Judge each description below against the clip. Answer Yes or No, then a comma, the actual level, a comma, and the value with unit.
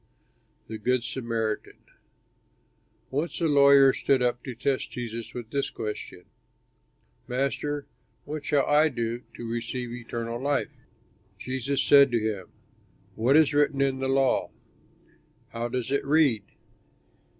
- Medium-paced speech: No, slow, 130 wpm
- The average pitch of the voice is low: Yes, low, 130 Hz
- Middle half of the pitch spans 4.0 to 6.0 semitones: No, average, 3.2 semitones